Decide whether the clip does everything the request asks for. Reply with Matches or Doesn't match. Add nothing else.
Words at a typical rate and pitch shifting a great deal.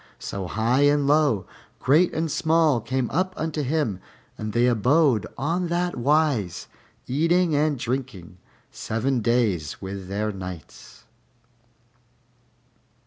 Doesn't match